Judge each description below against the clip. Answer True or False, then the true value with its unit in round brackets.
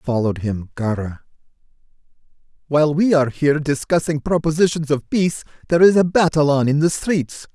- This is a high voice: False (150 Hz)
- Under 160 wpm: True (150 wpm)